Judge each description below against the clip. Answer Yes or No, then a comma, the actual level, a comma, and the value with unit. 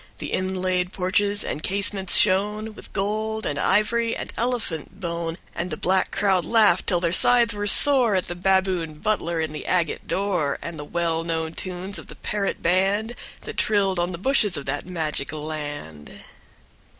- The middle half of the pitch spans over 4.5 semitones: No, average, 3.6 semitones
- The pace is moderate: Yes, average, 175 wpm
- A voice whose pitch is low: No, medium, 185 Hz